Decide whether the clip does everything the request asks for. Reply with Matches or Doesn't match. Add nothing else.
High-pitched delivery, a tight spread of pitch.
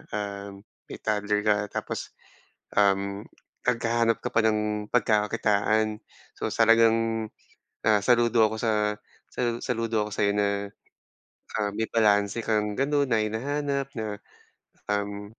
Doesn't match